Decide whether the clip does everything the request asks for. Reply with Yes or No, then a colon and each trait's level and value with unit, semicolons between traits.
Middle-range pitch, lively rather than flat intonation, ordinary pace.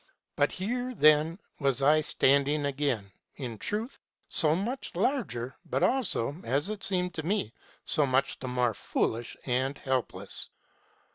Yes: medium, 145 Hz; wide, 6.2 semitones; average, 145 wpm